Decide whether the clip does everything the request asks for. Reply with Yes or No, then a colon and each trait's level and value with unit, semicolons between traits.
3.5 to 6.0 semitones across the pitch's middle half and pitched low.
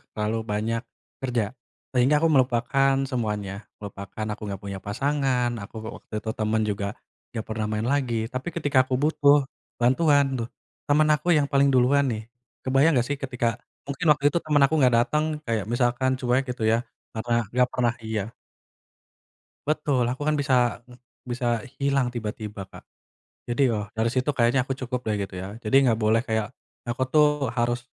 Yes: average, 3.8 semitones; low, 125 Hz